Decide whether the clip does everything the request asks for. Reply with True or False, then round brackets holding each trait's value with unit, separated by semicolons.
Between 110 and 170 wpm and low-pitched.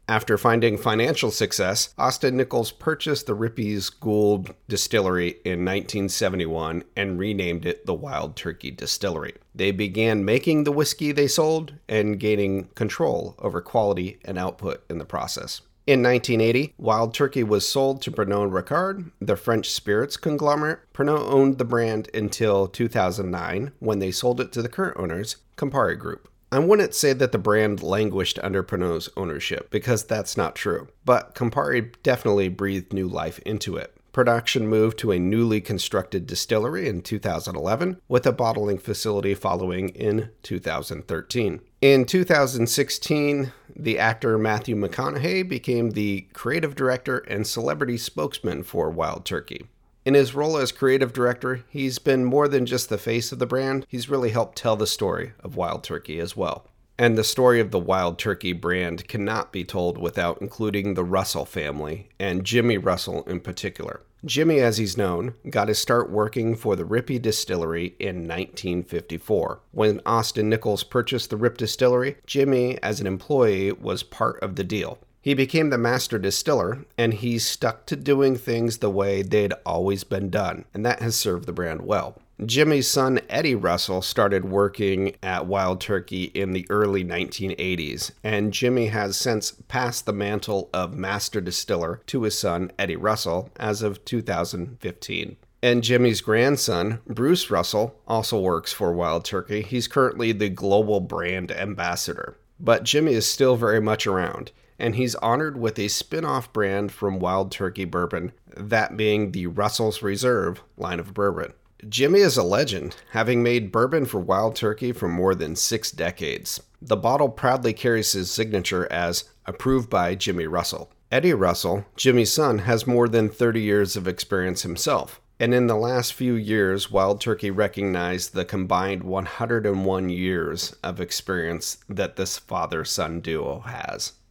True (160 wpm; 110 Hz)